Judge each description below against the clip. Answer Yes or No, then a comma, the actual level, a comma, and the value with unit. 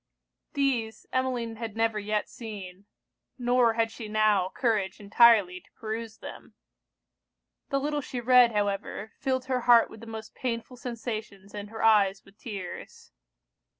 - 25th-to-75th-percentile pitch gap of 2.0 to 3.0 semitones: Yes, average, 2.7 semitones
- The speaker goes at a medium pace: Yes, average, 145 wpm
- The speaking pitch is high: Yes, high, 225 Hz